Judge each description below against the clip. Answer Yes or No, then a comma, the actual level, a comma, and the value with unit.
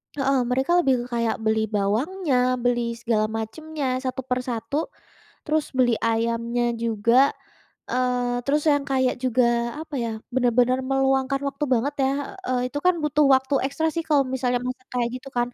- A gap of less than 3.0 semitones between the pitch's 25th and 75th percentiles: Yes, narrow, 2.5 semitones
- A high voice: Yes, very high, 255 Hz